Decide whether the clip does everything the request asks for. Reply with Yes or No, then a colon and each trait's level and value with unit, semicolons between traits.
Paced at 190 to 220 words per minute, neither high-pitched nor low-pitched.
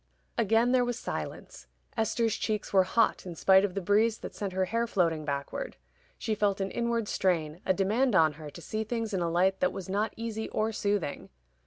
No: fast, 205 wpm; high, 205 Hz